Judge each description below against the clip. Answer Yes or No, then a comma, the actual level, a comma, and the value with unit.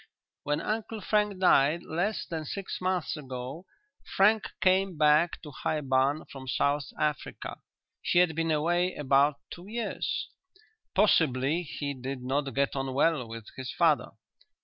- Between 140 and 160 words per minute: Yes, average, 145 wpm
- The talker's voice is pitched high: No, medium, 150 Hz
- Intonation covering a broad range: No, average, 4.8 semitones